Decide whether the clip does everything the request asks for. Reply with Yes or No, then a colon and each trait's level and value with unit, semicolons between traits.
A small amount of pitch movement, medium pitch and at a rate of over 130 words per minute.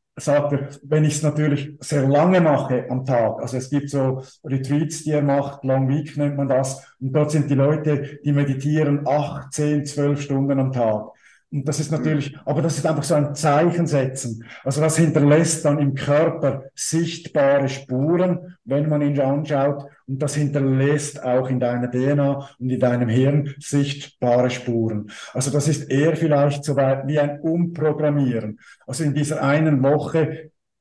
Yes: narrow, 1.9 semitones; medium, 145 Hz; average, 175 wpm